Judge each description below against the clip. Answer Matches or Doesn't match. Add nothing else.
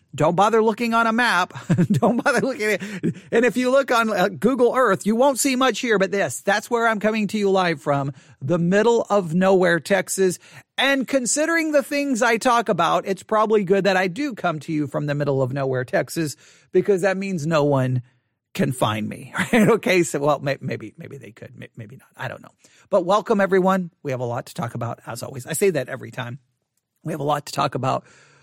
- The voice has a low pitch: Doesn't match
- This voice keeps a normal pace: Doesn't match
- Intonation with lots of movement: Matches